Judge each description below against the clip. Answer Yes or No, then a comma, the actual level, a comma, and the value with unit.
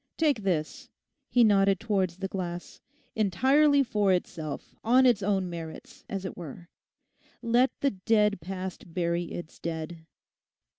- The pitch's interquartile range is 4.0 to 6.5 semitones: Yes, average, 4.5 semitones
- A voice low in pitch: No, high, 190 Hz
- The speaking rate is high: No, slow, 135 wpm